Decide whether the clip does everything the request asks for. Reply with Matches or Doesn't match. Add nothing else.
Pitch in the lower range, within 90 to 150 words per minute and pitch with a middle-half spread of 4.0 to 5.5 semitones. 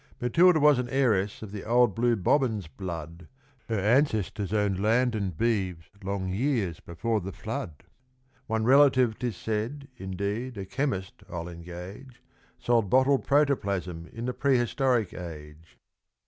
Matches